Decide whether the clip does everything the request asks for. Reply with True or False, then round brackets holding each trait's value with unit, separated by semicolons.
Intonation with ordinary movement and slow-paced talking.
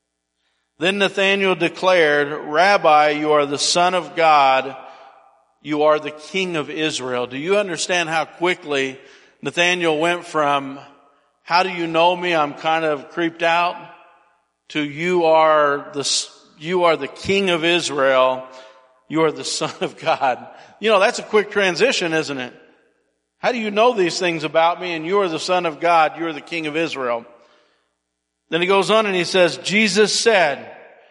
False (3.9 semitones; 170 wpm)